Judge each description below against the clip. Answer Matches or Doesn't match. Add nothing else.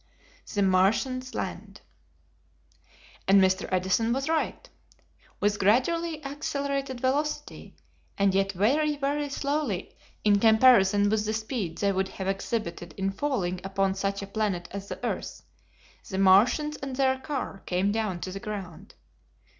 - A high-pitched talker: Matches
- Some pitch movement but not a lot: Doesn't match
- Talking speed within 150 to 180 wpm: Doesn't match